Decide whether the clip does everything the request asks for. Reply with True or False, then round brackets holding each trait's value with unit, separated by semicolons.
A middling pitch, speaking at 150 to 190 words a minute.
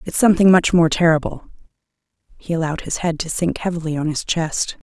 True (170 Hz; 185 wpm)